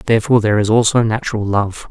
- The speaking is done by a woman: No, male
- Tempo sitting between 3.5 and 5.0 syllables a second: No, 7.0 syllables/s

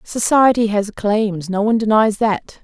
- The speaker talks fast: No, average, 160 wpm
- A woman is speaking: Yes, female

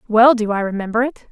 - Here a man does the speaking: No, female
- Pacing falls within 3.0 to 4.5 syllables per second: No, 6.1 syllables/s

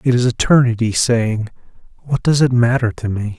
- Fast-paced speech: No, average, 175 wpm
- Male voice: Yes, male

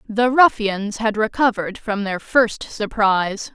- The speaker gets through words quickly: No, slow, 135 wpm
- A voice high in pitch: Yes, high, 215 Hz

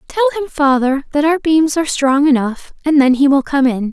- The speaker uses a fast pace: Yes, fast, 230 wpm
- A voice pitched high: Yes, very high, 280 Hz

